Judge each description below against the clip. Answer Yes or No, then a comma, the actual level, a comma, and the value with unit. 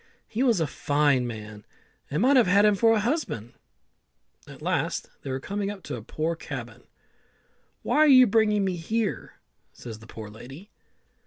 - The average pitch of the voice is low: No, medium, 180 Hz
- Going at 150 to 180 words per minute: Yes, average, 175 wpm